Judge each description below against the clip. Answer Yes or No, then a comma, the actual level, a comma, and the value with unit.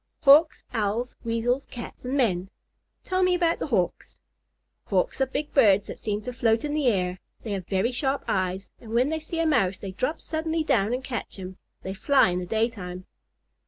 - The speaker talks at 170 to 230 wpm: Yes, average, 195 wpm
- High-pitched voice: Yes, high, 235 Hz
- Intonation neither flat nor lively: No, wide, 6.6 semitones